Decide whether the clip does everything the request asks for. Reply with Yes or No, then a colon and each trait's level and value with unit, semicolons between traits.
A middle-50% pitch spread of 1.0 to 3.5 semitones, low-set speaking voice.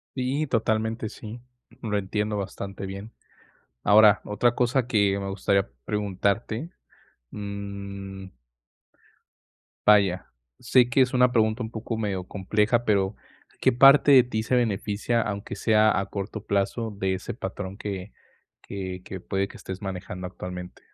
Yes: average, 2.8 semitones; low, 105 Hz